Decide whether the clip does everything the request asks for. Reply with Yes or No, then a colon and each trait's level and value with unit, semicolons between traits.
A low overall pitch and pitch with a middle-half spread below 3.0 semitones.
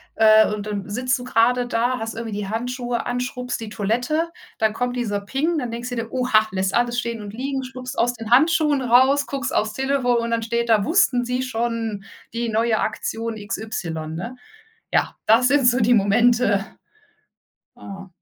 No: high, 235 Hz; narrow, 2.5 semitones